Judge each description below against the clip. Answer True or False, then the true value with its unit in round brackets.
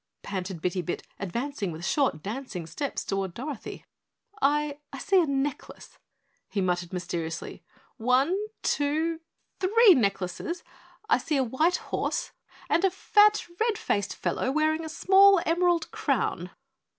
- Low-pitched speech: False (280 Hz)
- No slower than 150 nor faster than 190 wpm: False (135 wpm)